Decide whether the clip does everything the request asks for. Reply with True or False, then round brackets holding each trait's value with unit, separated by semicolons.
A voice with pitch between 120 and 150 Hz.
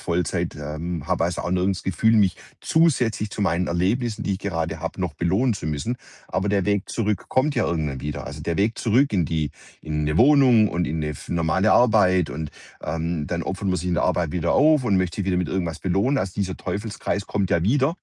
False (95 Hz)